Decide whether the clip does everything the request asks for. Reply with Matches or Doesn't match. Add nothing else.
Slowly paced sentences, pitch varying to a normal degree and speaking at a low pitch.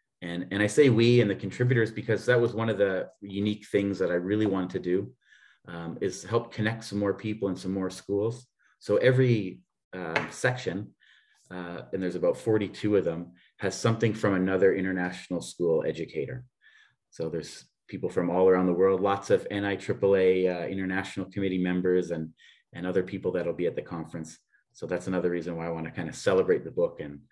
Doesn't match